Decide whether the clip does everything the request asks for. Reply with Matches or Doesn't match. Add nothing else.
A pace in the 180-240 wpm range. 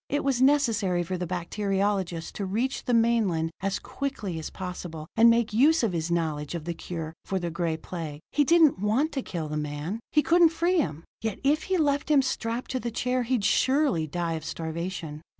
Matches